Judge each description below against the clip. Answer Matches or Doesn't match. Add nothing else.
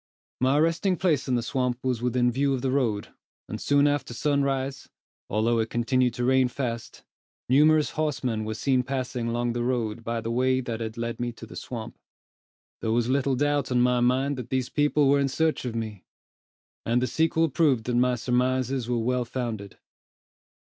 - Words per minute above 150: Matches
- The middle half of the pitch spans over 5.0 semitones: Doesn't match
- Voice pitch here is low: Matches